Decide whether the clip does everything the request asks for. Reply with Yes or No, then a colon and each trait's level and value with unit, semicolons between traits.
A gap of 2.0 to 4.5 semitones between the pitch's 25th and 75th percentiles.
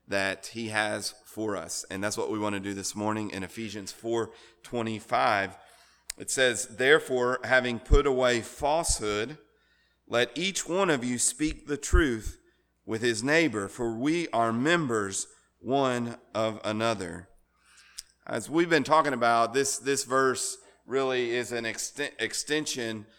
Yes: average, 3.9 semitones